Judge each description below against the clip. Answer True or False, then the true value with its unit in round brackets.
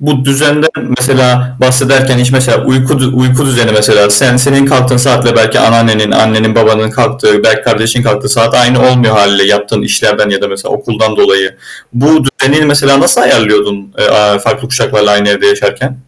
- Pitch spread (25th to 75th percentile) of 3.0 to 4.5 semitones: True (3.9 semitones)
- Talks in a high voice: False (125 Hz)